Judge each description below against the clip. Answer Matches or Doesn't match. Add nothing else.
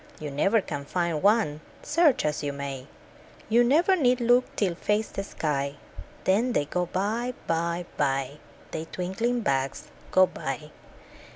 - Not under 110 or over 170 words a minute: Matches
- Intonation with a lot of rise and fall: Matches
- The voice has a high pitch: Doesn't match